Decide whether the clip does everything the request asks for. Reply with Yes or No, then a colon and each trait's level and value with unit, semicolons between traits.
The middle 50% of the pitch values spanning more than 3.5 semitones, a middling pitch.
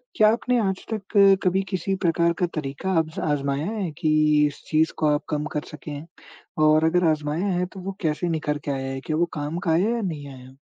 Yes: average, 4.0 semitones; medium, 160 Hz